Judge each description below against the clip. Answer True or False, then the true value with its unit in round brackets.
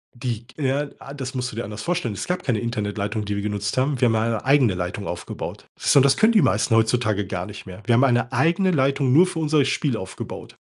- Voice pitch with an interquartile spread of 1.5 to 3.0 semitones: False (4.8 semitones)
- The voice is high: False (120 Hz)